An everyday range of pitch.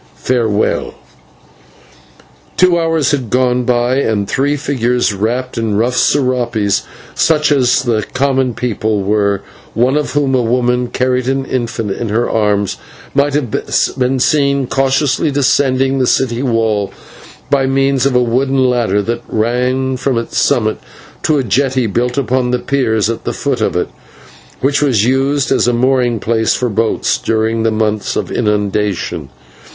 Yes: average, 3.1 semitones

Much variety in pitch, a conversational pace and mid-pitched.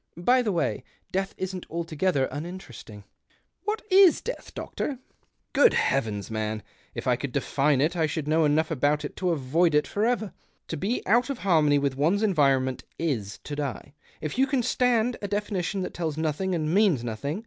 Yes: wide, 6.0 semitones; average, 190 wpm; medium, 165 Hz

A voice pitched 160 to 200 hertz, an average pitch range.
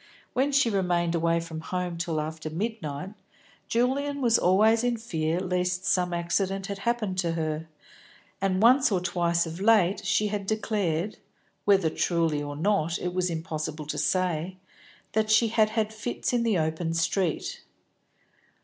Yes: medium, 185 Hz; average, 4.5 semitones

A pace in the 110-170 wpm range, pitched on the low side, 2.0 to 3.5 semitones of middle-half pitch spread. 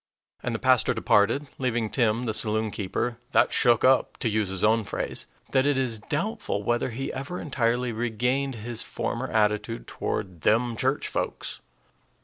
Yes: average, 155 wpm; low, 115 Hz; average, 3.2 semitones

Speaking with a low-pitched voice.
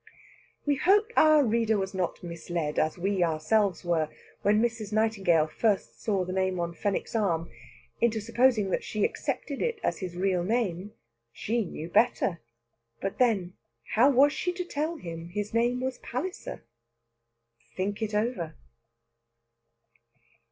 No: high, 205 Hz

